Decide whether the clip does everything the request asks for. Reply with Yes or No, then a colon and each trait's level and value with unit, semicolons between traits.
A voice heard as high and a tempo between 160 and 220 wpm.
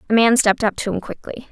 No: high, 225 Hz; fast, 275 wpm